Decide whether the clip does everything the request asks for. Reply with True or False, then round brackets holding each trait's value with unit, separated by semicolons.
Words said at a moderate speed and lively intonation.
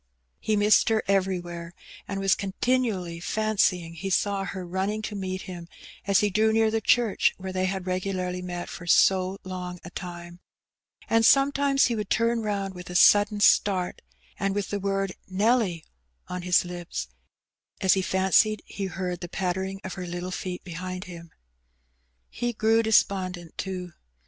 False (165 wpm; 2.5 semitones)